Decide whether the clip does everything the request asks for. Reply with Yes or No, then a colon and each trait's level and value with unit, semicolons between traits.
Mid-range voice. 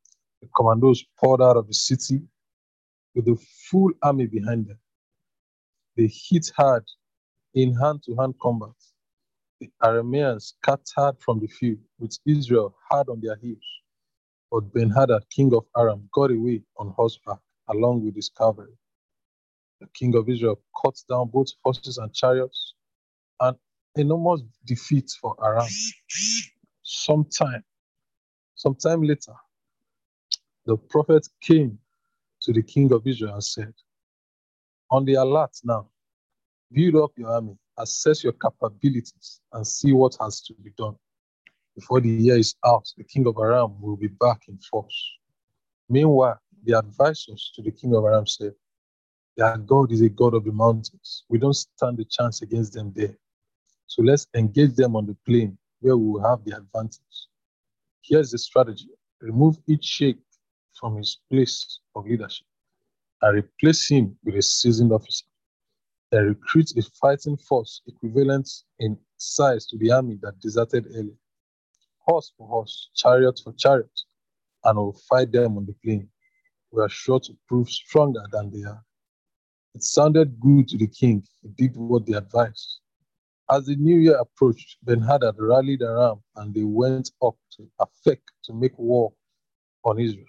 No: low, 120 Hz